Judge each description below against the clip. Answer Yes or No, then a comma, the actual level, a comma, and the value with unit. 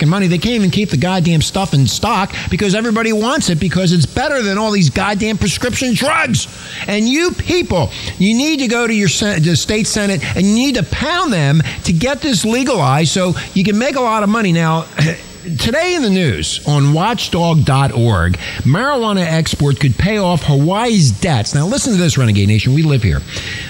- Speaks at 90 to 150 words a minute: No, average, 200 wpm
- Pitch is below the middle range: No, medium, 180 Hz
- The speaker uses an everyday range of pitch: No, wide, 6.8 semitones